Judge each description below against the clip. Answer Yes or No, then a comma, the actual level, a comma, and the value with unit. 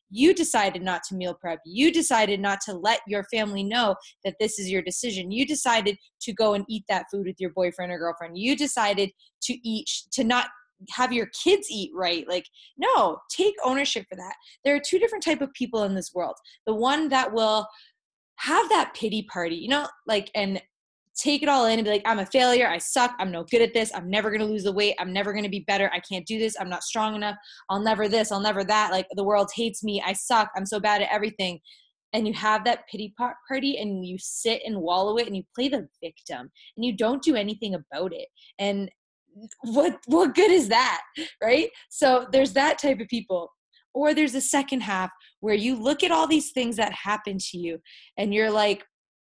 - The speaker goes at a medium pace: No, fast, 225 wpm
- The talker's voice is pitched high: Yes, high, 215 Hz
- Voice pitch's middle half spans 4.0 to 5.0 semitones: Yes, average, 4.6 semitones